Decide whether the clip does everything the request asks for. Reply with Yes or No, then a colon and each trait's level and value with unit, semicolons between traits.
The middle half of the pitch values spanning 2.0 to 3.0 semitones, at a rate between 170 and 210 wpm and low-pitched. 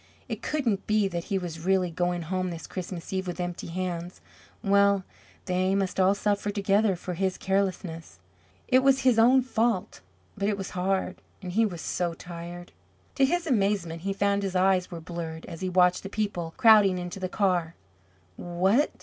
No: narrow, 2.4 semitones; average, 180 wpm; high, 190 Hz